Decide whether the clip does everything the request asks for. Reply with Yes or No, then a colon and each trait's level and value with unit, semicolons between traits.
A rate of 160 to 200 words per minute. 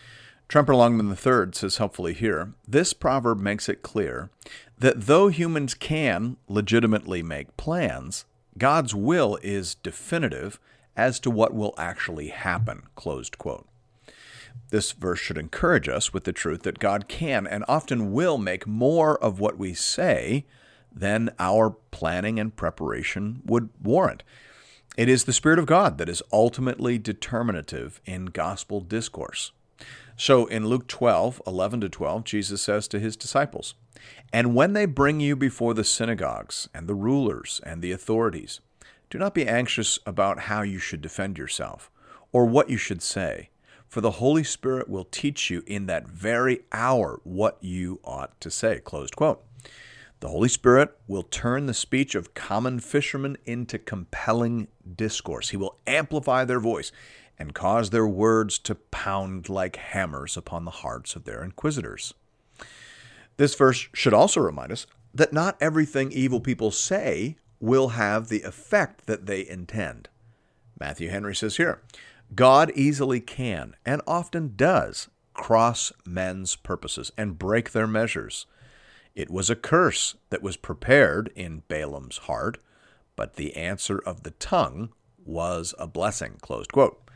No: average, 150 wpm